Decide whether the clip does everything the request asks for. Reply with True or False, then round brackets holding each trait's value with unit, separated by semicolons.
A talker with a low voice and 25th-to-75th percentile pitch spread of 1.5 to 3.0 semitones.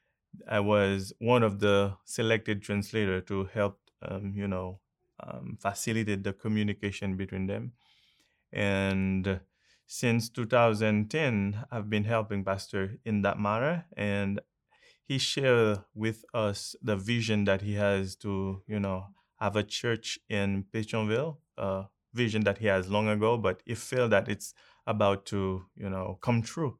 True (105 Hz; 2.4 semitones)